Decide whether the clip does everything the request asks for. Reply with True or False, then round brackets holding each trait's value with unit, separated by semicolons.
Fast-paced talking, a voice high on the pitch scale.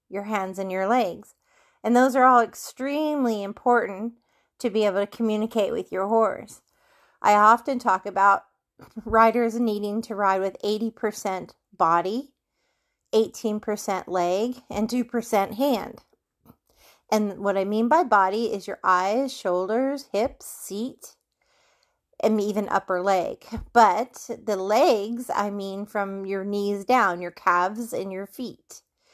False (135 wpm; 215 Hz)